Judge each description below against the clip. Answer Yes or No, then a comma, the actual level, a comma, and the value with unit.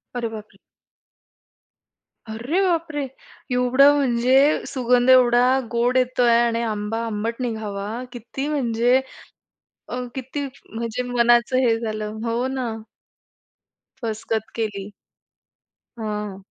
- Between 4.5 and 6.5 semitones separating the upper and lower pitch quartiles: No, narrow, 2.4 semitones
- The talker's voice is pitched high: Yes, high, 235 Hz